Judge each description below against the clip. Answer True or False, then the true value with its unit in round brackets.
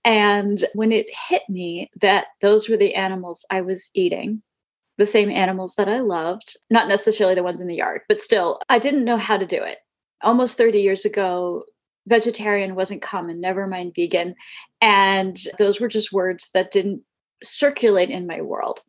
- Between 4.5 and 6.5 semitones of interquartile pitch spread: False (3.1 semitones)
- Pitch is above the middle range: True (205 Hz)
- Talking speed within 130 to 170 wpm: False (180 wpm)